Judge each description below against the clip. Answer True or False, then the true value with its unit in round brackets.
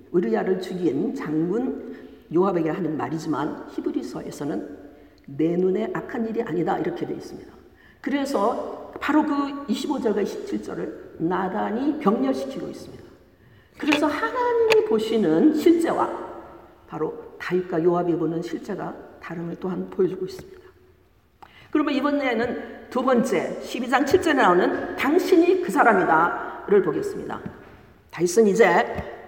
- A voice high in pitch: True (250 Hz)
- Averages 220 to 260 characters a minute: False (285 characters per minute)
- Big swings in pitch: True (9.0 semitones)